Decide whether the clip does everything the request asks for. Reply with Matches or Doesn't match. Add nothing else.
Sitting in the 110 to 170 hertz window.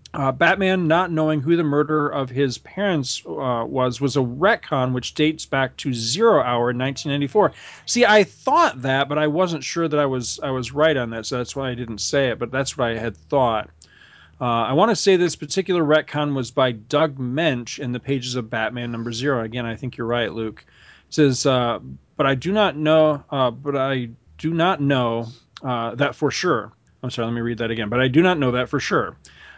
Matches